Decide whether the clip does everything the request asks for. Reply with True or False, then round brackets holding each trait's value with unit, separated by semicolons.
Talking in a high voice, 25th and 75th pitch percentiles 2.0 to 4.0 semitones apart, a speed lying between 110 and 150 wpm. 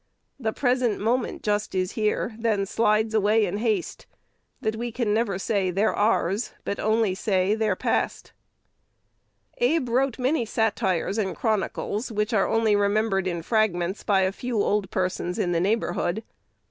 False (215 Hz; 2.7 semitones; 160 wpm)